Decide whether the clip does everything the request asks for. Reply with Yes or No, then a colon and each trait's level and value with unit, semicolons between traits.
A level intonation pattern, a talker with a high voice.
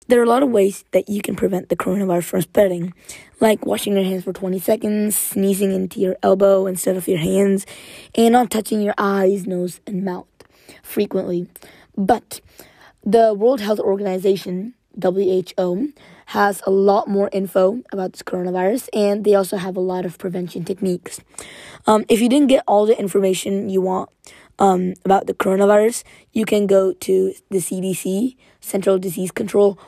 Yes: narrow, 2.0 semitones; high, 195 Hz